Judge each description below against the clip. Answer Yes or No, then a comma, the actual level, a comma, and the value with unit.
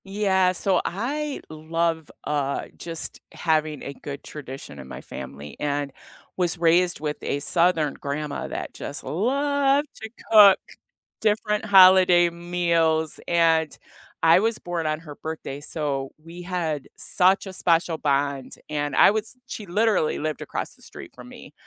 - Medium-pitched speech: Yes, medium, 165 Hz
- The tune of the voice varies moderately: Yes, average, 4.0 semitones